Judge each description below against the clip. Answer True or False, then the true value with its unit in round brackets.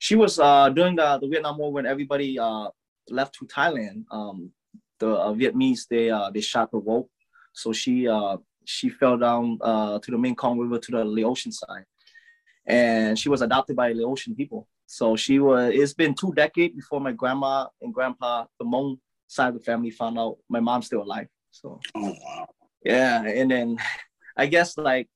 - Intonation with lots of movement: True (6.5 semitones)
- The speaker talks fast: False (185 wpm)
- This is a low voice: True (130 Hz)